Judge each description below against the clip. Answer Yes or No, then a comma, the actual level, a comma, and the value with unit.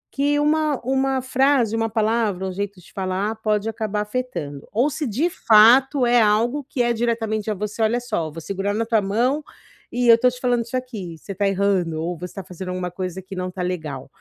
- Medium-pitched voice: No, high, 215 Hz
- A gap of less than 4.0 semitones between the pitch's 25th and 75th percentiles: No, average, 4.6 semitones